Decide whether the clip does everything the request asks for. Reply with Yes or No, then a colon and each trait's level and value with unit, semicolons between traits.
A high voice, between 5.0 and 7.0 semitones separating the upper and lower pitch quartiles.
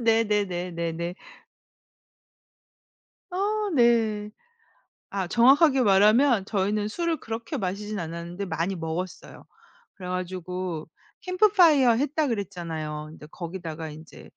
Yes: high, 200 Hz; wide, 5.5 semitones